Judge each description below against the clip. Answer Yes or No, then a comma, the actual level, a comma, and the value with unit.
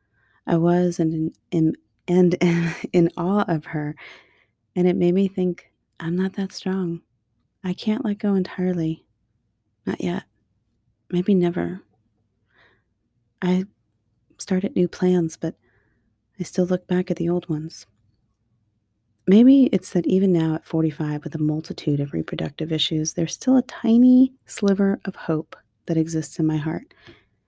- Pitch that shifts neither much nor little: No, wide, 7.7 semitones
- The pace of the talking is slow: No, average, 150 wpm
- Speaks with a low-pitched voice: No, medium, 165 Hz